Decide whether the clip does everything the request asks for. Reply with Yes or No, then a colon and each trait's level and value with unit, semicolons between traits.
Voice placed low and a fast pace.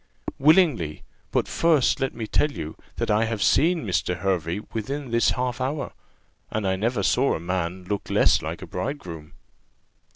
No: low, 110 Hz; average, 165 wpm